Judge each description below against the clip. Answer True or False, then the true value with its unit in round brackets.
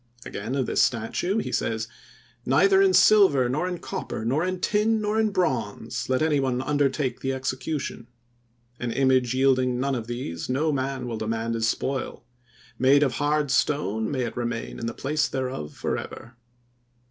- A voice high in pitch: False (130 Hz)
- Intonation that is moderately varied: True (4.0 semitones)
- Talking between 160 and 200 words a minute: True (170 wpm)